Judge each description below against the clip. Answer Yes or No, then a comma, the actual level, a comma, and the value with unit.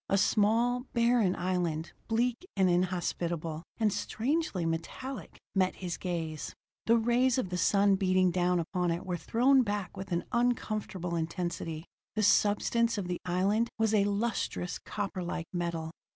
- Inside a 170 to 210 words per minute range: No, average, 145 wpm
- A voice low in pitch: No, high, 190 Hz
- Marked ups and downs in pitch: No, average, 4.4 semitones